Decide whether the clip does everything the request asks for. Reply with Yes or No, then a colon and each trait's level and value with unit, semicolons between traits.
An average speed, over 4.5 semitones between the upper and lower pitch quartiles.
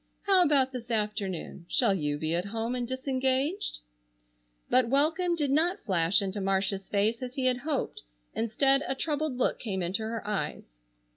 Yes: average, 165 wpm; wide, 5.5 semitones